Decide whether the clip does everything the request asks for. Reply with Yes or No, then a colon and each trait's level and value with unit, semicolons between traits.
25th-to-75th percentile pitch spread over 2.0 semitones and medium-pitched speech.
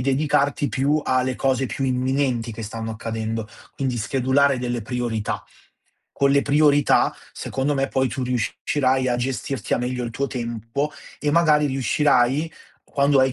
No: narrow, 2.5 semitones; low, 130 Hz